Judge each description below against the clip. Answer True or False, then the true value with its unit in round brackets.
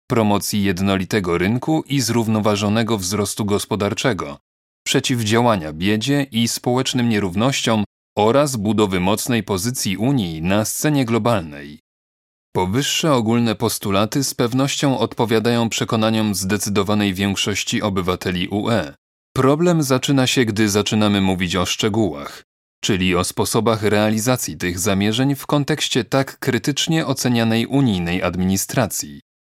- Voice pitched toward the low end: True (110 Hz)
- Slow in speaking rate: True (105 wpm)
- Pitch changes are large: False (4.5 semitones)